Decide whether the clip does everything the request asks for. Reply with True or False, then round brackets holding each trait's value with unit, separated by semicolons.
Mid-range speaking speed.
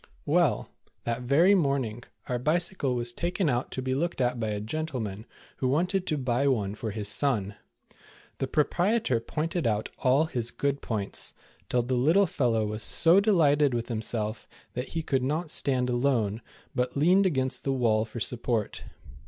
True (170 wpm)